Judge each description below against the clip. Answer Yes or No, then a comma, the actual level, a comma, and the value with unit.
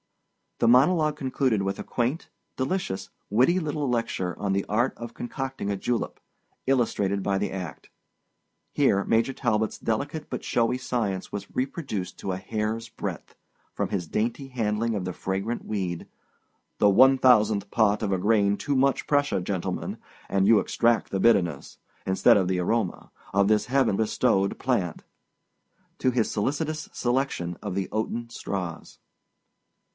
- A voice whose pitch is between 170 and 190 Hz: No, low, 110 Hz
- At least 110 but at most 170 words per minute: Yes, average, 145 wpm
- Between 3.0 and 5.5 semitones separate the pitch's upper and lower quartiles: Yes, average, 4.7 semitones